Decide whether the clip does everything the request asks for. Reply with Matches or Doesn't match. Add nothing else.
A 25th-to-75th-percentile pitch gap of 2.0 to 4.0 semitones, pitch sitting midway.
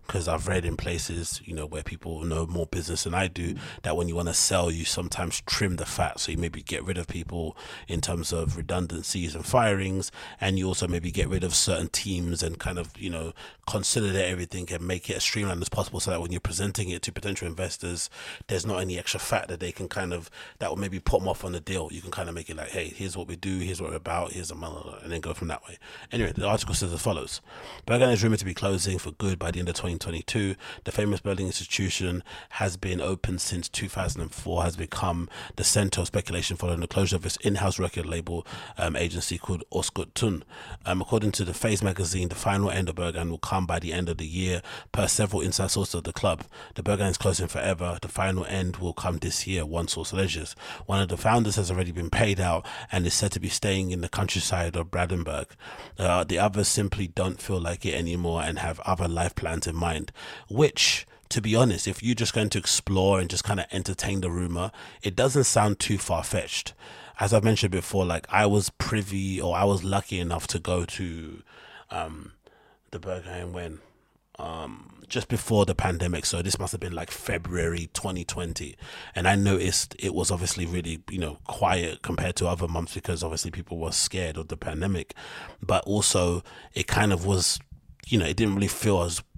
Doesn't match